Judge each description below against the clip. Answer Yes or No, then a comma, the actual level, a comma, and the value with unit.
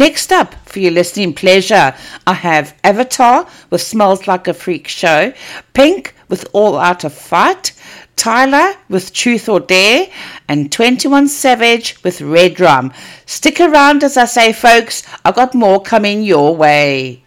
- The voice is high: Yes, high, 210 Hz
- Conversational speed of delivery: Yes, average, 155 wpm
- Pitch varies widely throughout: Yes, wide, 6.7 semitones